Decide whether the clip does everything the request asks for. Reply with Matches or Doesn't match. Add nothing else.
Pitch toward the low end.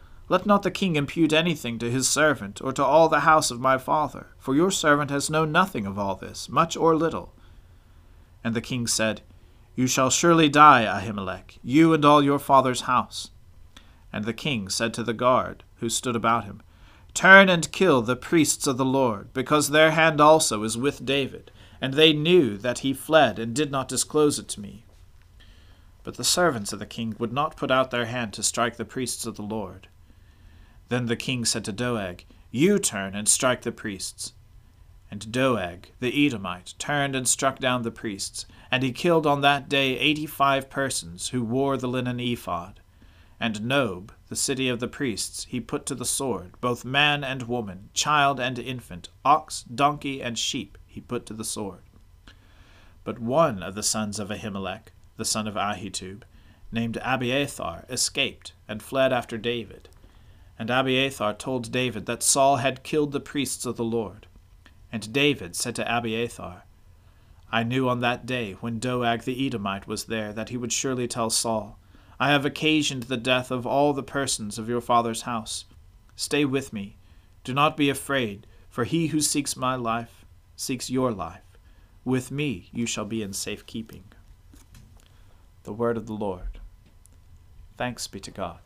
Matches